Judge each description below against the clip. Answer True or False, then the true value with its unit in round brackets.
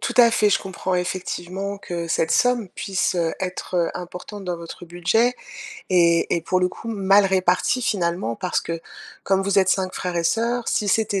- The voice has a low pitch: False (185 Hz)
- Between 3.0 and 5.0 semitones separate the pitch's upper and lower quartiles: False (2.5 semitones)